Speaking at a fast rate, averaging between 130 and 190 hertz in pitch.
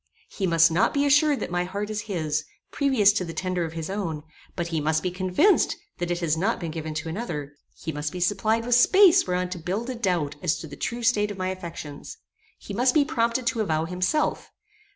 Yes: fast, 225 wpm; medium, 185 Hz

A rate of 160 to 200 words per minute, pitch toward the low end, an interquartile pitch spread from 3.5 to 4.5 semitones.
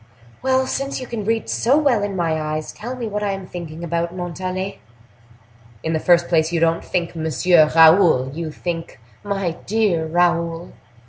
No: average, 175 wpm; medium, 175 Hz; average, 3.8 semitones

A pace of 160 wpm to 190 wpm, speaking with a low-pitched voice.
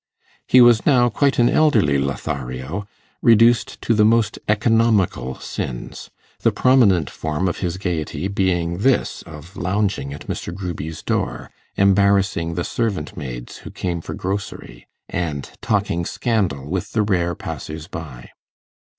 No: slow, 135 wpm; very low, 90 Hz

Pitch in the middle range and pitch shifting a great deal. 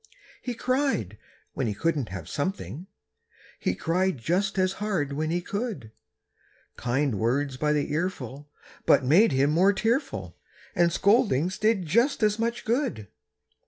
Yes: medium, 170 Hz; wide, 7.4 semitones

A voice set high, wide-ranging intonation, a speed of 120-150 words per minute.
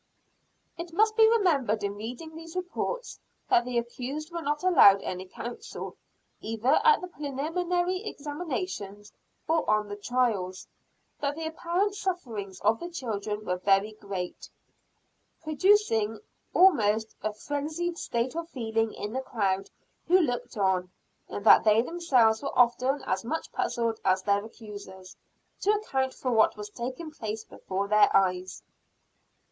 Yes: high, 245 Hz; wide, 7.8 semitones; average, 140 wpm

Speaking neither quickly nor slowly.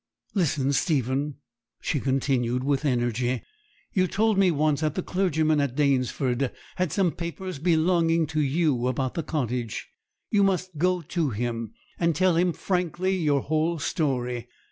Yes: average, 145 wpm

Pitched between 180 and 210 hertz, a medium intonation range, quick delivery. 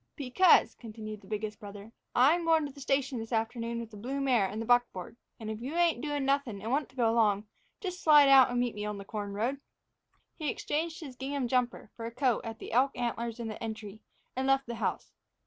No: high, 240 Hz; average, 3.9 semitones; fast, 230 wpm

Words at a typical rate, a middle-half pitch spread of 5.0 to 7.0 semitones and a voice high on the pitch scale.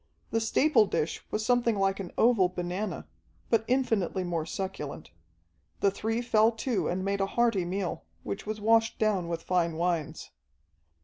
No: average, 160 wpm; average, 4.0 semitones; high, 200 Hz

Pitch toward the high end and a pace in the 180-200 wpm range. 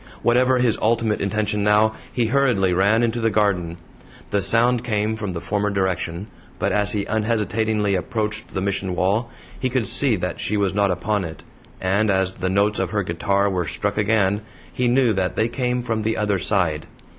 No: low, 105 Hz; average, 190 wpm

